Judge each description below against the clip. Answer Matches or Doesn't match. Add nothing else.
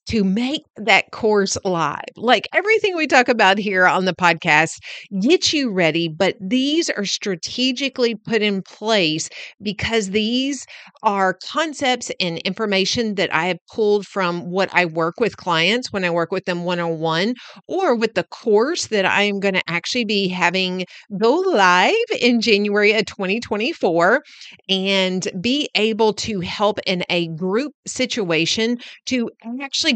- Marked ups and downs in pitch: Doesn't match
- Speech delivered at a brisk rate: Doesn't match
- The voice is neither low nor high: Doesn't match